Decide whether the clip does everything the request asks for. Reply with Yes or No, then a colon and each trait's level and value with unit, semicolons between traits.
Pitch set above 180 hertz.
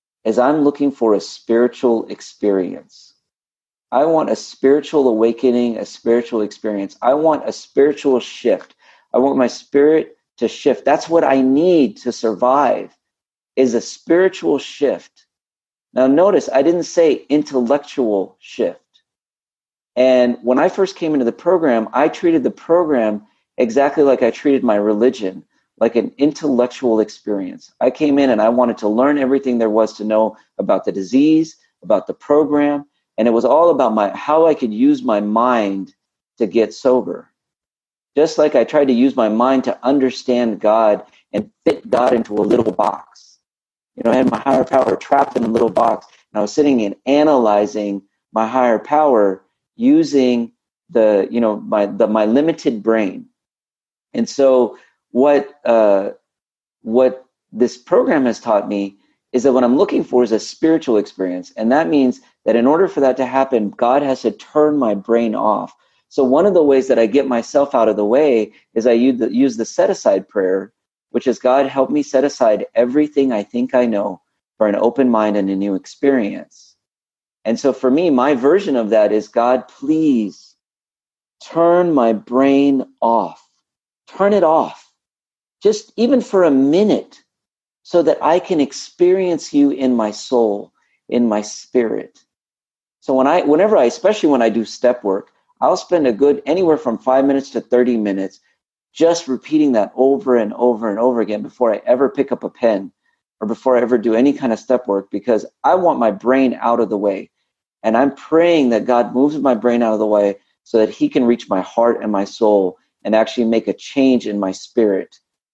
No: low, 125 Hz